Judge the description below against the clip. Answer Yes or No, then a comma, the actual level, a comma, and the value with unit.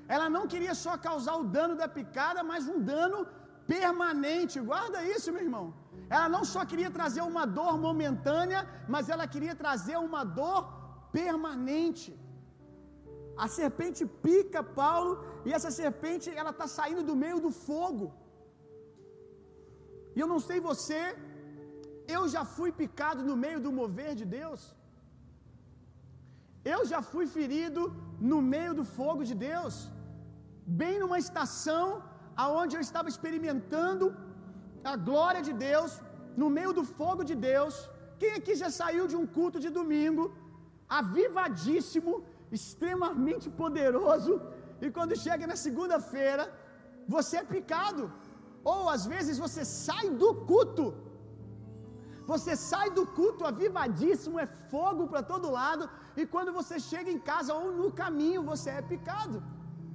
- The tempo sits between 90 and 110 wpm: No, average, 135 wpm